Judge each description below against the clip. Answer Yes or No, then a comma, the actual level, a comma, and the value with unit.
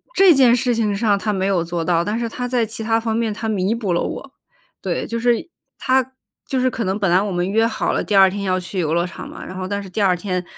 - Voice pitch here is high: Yes, high, 205 Hz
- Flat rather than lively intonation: No, average, 3.8 semitones